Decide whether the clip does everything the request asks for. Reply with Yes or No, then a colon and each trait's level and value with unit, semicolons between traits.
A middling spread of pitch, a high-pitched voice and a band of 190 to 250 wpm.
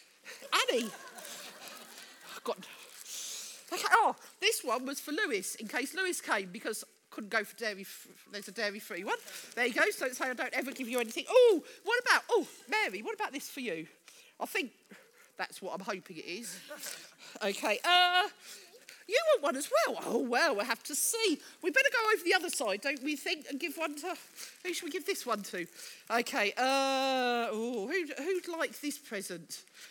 No: wide, 8.0 semitones; very high, 300 Hz; average, 195 wpm